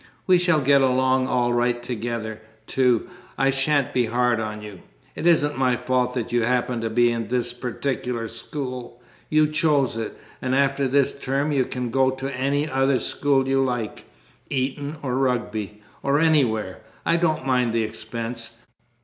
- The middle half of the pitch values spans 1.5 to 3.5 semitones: Yes, narrow, 2.6 semitones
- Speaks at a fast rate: No, average, 165 wpm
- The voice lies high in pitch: No, low, 125 Hz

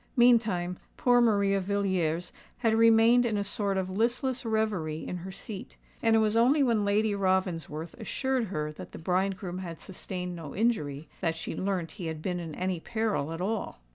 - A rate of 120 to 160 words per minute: No, average, 180 wpm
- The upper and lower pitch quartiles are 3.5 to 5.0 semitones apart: Yes, average, 4.2 semitones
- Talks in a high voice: Yes, high, 195 Hz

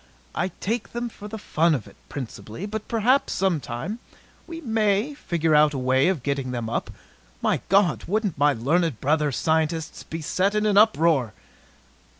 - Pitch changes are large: Yes, wide, 6.7 semitones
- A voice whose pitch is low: No, medium, 170 Hz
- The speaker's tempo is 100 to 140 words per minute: No, average, 165 wpm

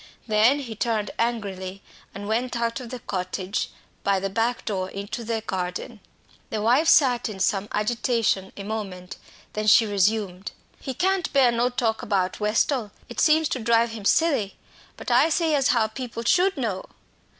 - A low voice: No, high, 225 Hz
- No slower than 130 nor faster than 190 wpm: Yes, average, 170 wpm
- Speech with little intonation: No, average, 3.7 semitones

